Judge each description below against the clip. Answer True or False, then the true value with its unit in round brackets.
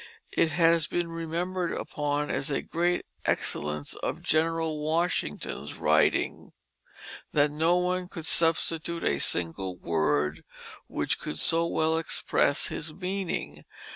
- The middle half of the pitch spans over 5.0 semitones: False (2.8 semitones)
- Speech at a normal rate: False (120 wpm)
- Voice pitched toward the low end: False (160 Hz)